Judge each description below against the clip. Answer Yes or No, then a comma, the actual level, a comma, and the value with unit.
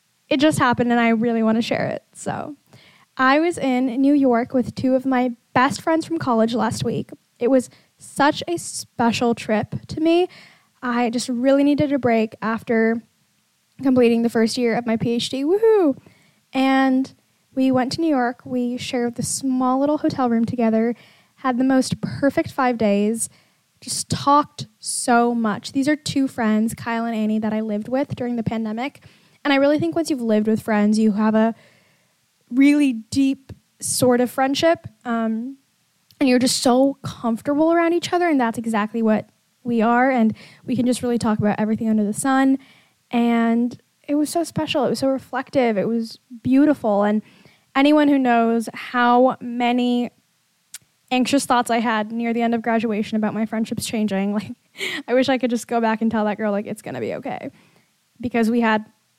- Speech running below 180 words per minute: No, average, 185 wpm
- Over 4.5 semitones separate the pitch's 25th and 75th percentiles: No, average, 3.0 semitones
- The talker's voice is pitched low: No, high, 245 Hz